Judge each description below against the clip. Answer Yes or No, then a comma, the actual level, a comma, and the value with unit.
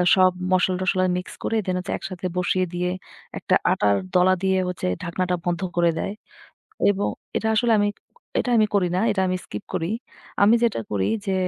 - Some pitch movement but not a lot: No, narrow, 1.6 semitones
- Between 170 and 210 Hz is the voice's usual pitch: Yes, medium, 185 Hz